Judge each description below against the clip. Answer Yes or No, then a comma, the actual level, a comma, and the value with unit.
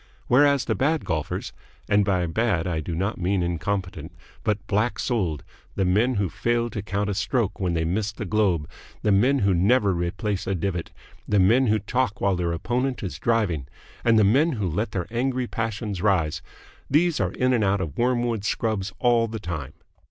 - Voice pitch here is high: No, low, 100 Hz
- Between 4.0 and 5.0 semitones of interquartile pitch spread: Yes, average, 4.6 semitones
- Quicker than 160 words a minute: Yes, average, 190 wpm